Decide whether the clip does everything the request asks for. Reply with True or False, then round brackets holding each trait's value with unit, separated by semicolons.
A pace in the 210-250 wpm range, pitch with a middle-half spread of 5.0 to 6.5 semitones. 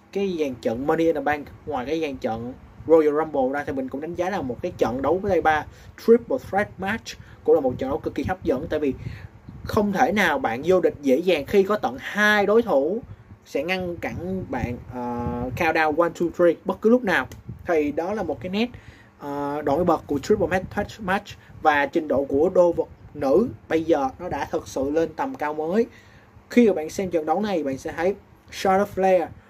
True (225 wpm; 5.3 semitones)